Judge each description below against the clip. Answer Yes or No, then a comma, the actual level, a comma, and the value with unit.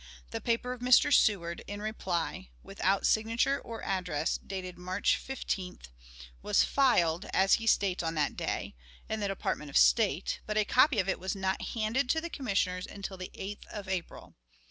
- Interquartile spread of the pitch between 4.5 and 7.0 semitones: No, average, 3.6 semitones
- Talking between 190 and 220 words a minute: No, average, 175 wpm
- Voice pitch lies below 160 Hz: No, high, 195 Hz